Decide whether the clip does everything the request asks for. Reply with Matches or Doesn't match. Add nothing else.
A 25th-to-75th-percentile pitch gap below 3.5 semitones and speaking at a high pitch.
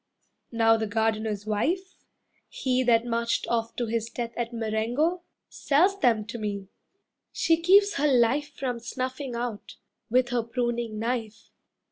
Matches